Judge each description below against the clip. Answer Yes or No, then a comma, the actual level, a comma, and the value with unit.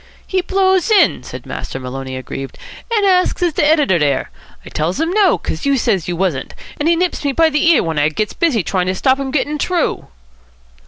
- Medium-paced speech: No, fast, 210 wpm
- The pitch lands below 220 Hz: No, very high, 280 Hz